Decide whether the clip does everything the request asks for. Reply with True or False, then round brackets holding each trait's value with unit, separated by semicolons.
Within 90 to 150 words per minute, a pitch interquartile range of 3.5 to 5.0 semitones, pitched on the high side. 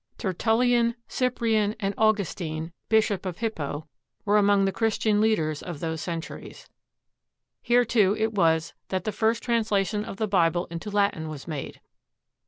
True (145 wpm; 4.6 semitones; 205 Hz)